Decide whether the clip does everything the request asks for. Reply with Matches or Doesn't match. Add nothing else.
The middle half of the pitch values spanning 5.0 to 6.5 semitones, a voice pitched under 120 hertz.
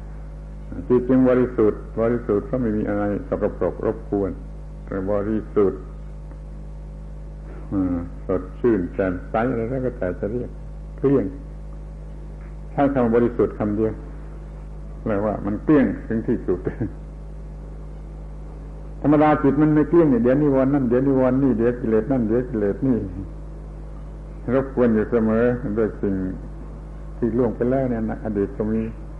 Doesn't match